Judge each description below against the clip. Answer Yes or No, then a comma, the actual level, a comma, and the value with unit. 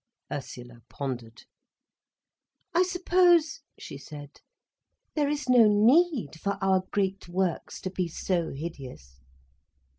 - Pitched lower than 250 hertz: Yes, high, 190 Hz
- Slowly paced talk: Yes, slow, 115 wpm